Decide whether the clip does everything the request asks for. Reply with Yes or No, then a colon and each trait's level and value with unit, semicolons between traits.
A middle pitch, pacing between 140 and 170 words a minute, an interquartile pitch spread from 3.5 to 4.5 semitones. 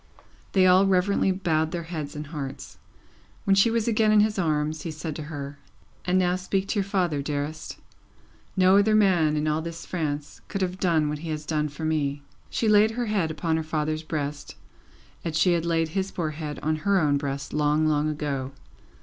No: medium, 160 Hz; average, 200 wpm; average, 3.8 semitones